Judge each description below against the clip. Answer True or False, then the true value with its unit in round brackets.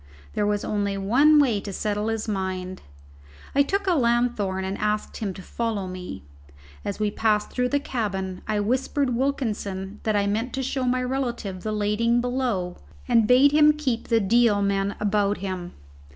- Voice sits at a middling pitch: False (215 Hz)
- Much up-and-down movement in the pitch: False (4.0 semitones)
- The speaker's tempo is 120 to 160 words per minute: False (175 wpm)